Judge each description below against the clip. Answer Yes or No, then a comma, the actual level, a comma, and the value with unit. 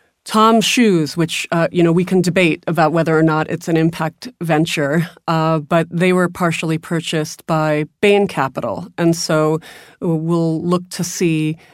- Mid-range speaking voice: Yes, medium, 165 Hz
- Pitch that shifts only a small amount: Yes, narrow, 1.9 semitones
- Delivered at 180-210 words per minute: No, average, 165 wpm